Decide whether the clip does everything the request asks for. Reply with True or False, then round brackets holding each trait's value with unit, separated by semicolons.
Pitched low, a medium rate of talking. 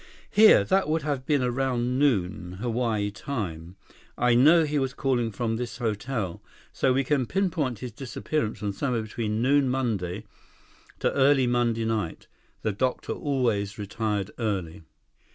True (120 Hz; 145 wpm)